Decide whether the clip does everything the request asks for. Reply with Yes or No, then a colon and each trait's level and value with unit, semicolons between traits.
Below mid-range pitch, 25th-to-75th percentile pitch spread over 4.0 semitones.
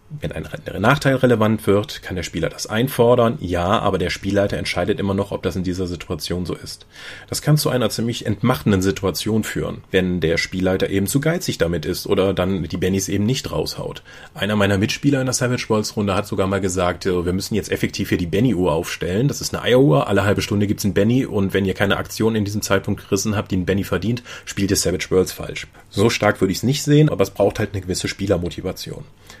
No: low, 100 Hz; average, 3.4 semitones